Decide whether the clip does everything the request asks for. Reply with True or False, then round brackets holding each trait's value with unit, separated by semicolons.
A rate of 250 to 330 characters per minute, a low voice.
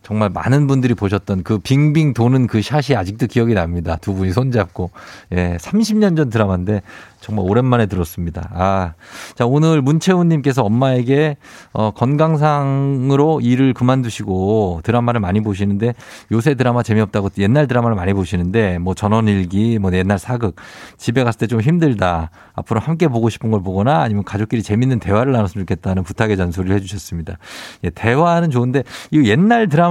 False (375 characters per minute; 110 Hz)